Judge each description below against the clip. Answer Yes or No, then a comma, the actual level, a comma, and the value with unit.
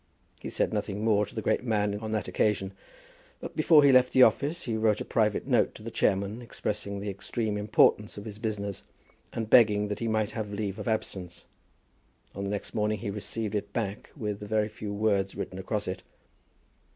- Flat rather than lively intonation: Yes, narrow, 1.5 semitones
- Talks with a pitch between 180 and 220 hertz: No, low, 105 Hz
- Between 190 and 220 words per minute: Yes, average, 200 wpm